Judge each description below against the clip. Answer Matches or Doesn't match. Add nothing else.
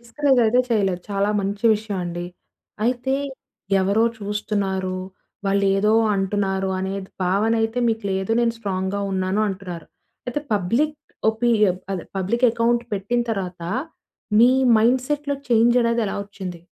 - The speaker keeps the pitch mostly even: Doesn't match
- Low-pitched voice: Doesn't match